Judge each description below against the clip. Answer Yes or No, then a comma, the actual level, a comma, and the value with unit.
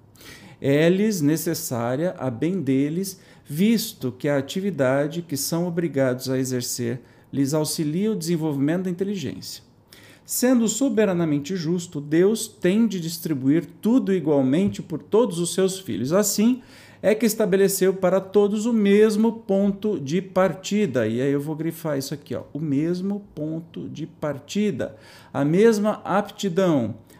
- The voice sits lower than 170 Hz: No, medium, 175 Hz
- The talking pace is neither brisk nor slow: Yes, average, 135 wpm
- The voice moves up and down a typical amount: No, wide, 5.7 semitones